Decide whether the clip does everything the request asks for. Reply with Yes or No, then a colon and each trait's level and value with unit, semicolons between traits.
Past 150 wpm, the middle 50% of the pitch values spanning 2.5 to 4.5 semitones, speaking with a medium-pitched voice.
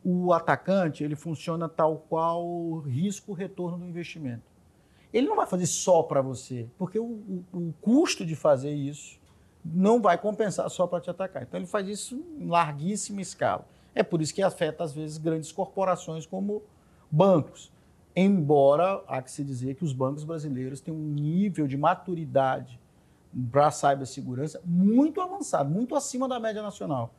No: average, 160 wpm; average, 4.9 semitones; medium, 165 Hz